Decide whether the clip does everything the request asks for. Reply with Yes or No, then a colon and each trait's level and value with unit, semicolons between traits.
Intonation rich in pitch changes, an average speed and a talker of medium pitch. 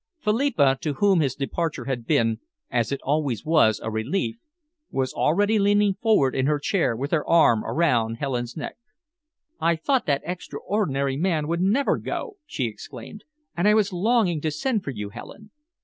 Yes: wide, 7.2 semitones; average, 170 wpm; medium, 155 Hz